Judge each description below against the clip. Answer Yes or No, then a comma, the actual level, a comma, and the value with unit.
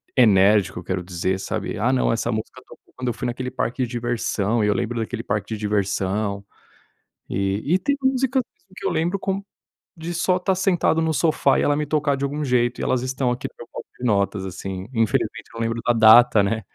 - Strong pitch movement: Yes, wide, 5.9 semitones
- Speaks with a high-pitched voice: No, low, 120 Hz